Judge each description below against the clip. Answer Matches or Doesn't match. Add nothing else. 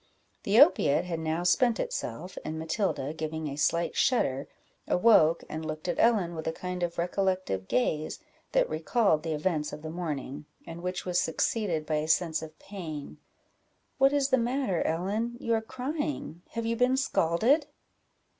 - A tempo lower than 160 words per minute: Doesn't match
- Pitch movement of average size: Doesn't match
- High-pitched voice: Doesn't match